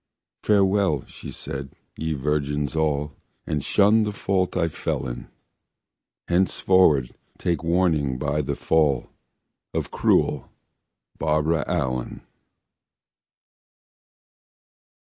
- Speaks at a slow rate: Yes, slow, 90 wpm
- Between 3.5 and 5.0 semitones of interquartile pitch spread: Yes, average, 4.2 semitones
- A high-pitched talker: No, very low, 75 Hz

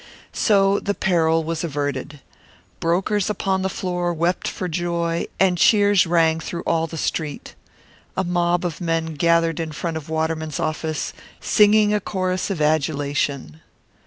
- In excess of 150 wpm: No, average, 145 wpm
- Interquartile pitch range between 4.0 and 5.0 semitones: No, average, 2.7 semitones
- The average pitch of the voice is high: No, medium, 170 Hz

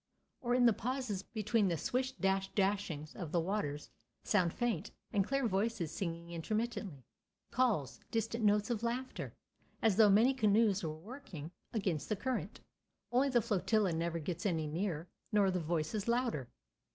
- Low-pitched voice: No, high, 205 Hz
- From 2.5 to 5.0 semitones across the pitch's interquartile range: No, wide, 5.4 semitones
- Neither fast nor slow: Yes, average, 150 wpm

